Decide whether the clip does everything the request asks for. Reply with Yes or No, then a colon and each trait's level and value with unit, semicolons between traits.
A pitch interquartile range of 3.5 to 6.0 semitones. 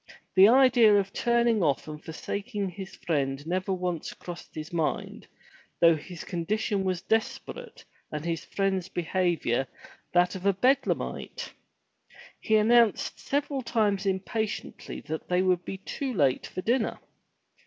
Yes: average, 4.3 semitones